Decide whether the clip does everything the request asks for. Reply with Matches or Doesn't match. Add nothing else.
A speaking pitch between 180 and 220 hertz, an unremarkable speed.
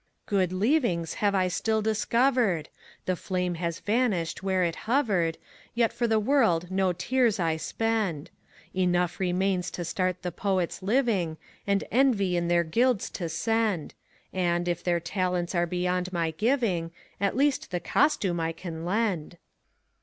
Matches